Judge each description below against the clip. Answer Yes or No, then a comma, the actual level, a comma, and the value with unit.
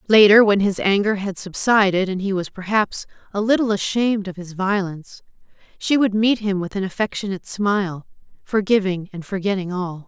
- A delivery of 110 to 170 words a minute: Yes, average, 165 wpm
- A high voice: Yes, high, 195 Hz